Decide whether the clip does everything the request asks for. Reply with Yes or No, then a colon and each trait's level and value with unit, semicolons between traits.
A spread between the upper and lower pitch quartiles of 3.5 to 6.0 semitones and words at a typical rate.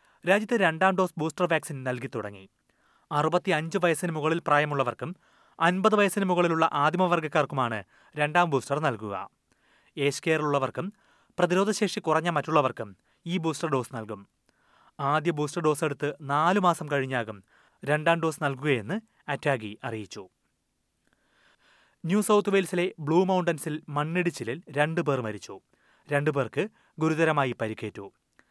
Yes: average, 4.4 semitones; average, 105 wpm